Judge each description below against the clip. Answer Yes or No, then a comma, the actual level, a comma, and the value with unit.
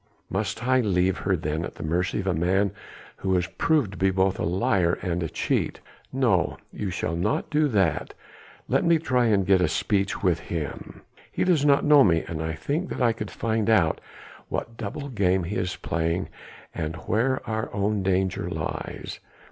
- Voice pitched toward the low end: Yes, very low, 95 Hz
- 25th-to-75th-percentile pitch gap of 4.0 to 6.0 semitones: Yes, average, 4.4 semitones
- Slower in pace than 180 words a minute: No, average, 190 wpm